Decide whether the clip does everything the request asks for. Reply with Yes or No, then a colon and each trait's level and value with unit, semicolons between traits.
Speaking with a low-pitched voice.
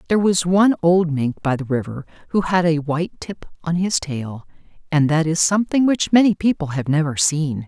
No: medium, 165 Hz